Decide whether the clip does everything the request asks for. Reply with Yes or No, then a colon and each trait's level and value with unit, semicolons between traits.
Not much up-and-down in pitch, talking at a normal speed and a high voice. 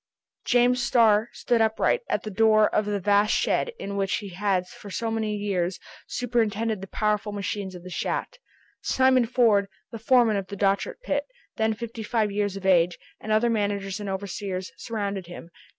Yes: narrow, 2.3 semitones; average, 180 wpm; high, 210 Hz